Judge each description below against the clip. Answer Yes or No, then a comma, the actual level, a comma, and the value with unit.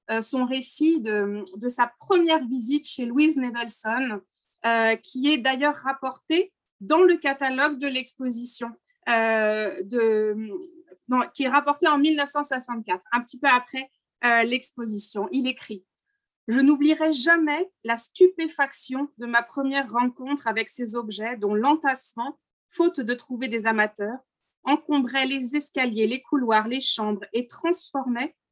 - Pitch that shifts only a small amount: No, average, 4.0 semitones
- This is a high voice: Yes, very high, 260 Hz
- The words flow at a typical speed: No, slow, 135 wpm